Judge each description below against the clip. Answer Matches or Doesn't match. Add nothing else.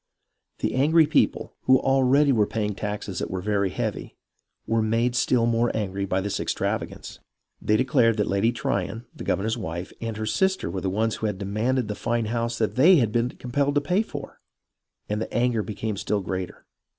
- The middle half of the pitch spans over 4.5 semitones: Doesn't match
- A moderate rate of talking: Matches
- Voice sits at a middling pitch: Doesn't match